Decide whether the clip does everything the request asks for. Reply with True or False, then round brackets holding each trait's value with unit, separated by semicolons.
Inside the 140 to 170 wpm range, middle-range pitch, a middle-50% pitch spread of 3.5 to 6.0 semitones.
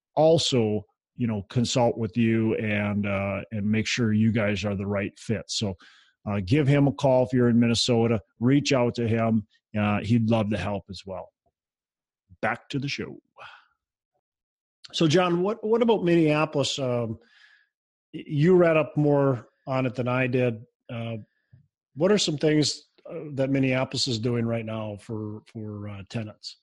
False (165 wpm; 120 Hz; 4.5 semitones)